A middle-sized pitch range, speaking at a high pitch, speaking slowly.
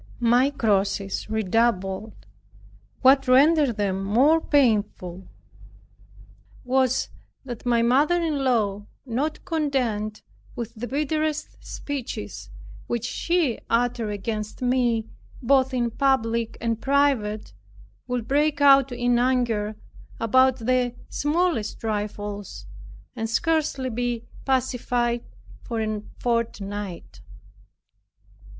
Yes: average, 3.8 semitones; high, 240 Hz; slow, 95 wpm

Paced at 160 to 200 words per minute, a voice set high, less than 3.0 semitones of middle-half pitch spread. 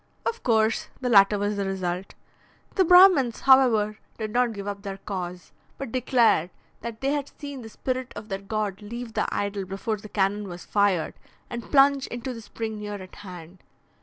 No: average, 185 wpm; high, 215 Hz; average, 3.9 semitones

